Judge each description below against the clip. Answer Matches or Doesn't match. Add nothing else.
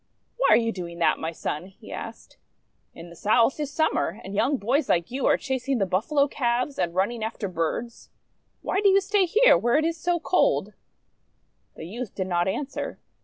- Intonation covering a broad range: Matches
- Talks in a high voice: Matches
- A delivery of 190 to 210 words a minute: Matches